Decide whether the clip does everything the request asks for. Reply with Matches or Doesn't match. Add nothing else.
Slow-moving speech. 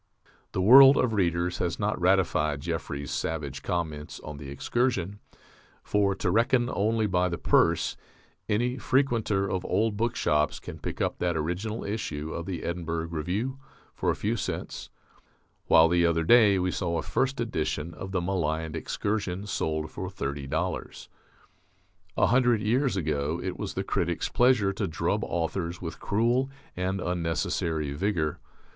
Doesn't match